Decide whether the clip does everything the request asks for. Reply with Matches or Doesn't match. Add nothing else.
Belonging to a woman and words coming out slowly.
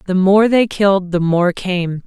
Doesn't match